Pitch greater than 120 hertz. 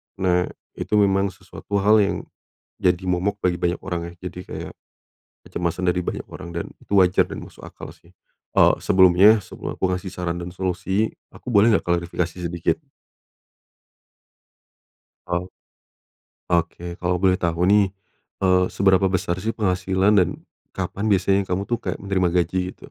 No: very low, 90 Hz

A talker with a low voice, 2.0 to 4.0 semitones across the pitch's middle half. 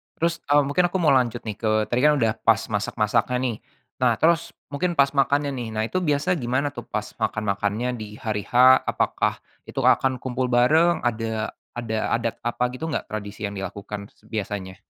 No: low, 120 Hz; average, 4.7 semitones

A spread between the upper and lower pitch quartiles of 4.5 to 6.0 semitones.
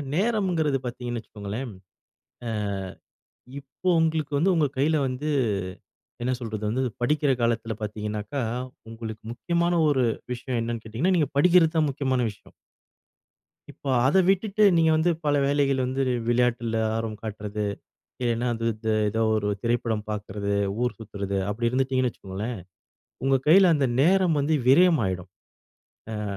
Yes: wide, 5.5 semitones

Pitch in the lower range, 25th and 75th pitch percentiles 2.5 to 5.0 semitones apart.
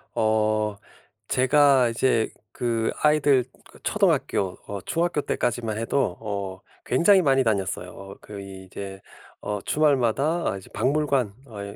No: low, 115 Hz; wide, 5.5 semitones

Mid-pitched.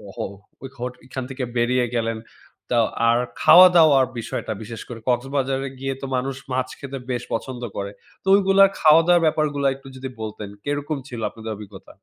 No: low, 130 Hz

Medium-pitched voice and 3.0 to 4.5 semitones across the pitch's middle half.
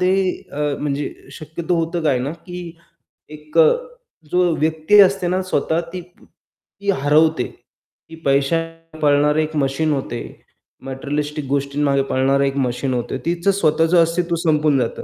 Yes: medium, 155 Hz; average, 3.3 semitones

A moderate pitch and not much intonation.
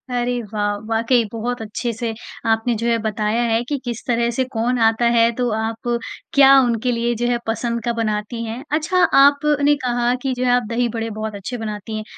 No: high, 235 Hz; narrow, 1.6 semitones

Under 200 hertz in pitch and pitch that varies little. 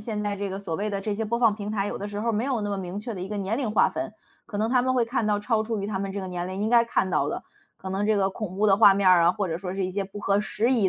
No: high, 205 Hz; narrow, 2.1 semitones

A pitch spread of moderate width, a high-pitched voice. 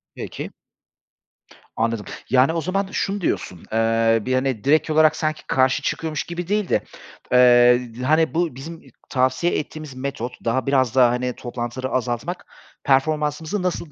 No: average, 4.3 semitones; low, 135 Hz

